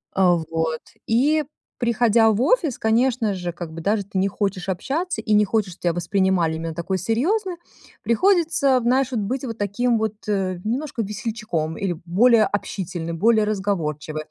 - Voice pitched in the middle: No, high, 210 Hz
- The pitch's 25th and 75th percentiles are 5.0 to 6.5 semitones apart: Yes, average, 5.3 semitones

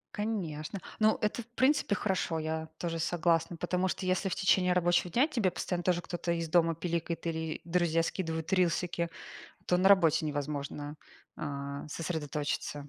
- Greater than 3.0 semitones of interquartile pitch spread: No, narrow, 2.5 semitones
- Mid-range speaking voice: Yes, medium, 170 Hz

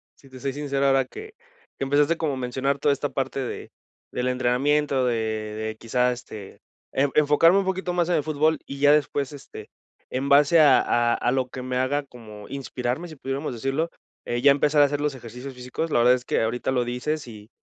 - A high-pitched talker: No, low, 135 Hz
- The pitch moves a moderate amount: Yes, average, 3.0 semitones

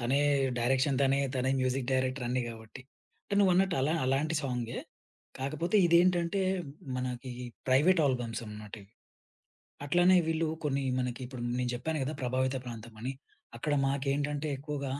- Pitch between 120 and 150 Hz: Yes, low, 135 Hz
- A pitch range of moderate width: Yes, average, 3.5 semitones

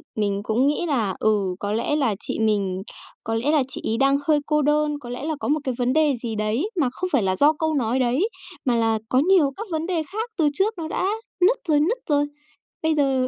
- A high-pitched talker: Yes, very high, 275 Hz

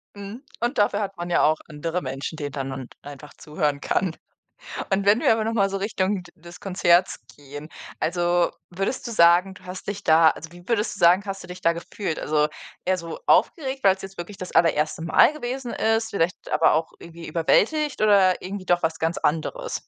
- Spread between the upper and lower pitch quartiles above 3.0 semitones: Yes, average, 3.7 semitones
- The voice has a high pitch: No, medium, 180 Hz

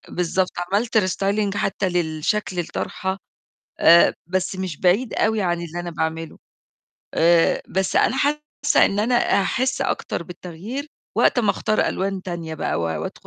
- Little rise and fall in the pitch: No, average, 3.6 semitones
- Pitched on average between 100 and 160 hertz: No, medium, 185 Hz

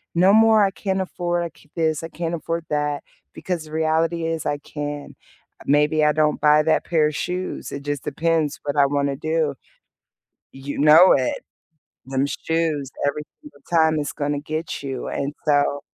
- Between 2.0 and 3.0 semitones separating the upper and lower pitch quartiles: Yes, narrow, 2.4 semitones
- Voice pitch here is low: No, medium, 155 Hz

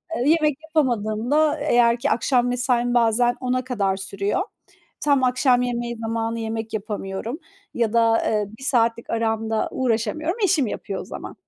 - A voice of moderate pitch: No, high, 235 Hz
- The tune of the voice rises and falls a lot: No, narrow, 2.4 semitones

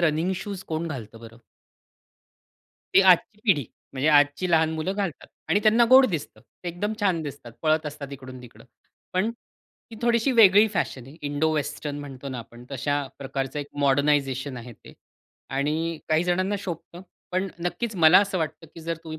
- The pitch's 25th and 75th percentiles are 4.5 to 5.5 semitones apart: Yes, average, 4.8 semitones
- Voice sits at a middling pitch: Yes, medium, 160 Hz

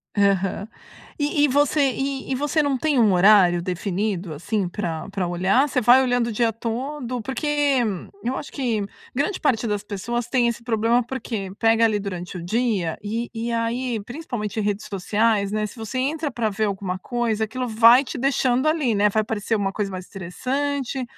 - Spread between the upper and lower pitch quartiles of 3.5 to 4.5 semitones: Yes, average, 4.1 semitones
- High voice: Yes, high, 225 Hz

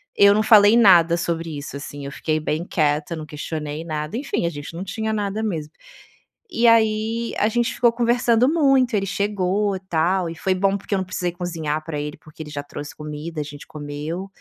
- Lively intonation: Yes, wide, 5.8 semitones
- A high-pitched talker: No, medium, 175 Hz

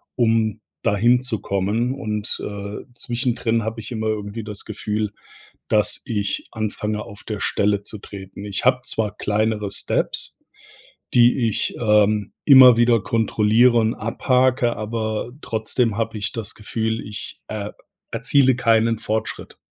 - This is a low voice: Yes, low, 110 Hz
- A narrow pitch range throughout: Yes, narrow, 1.9 semitones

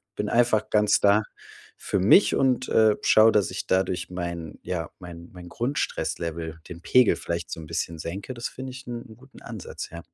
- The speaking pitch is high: No, low, 100 Hz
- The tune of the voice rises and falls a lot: Yes, wide, 5.7 semitones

